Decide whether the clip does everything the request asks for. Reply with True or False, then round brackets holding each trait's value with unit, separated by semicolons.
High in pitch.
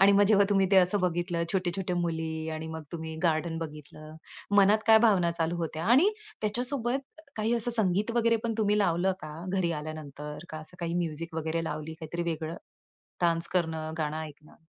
False (170 Hz)